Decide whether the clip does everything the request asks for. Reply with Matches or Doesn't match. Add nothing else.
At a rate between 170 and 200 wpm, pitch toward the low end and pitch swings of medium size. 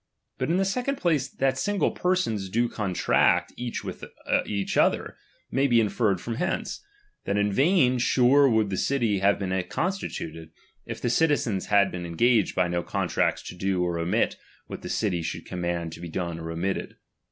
Doesn't match